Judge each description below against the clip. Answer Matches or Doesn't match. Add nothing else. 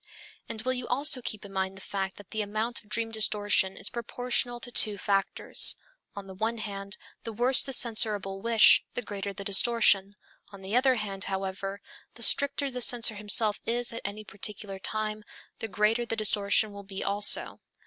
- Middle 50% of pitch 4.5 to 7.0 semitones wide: Doesn't match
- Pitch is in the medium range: Doesn't match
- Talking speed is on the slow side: Doesn't match